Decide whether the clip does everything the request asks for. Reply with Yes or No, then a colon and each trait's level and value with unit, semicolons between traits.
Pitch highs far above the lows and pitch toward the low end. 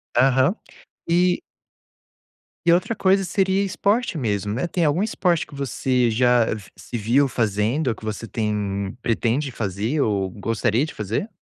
Yes: wide, 7.8 semitones; low, 125 Hz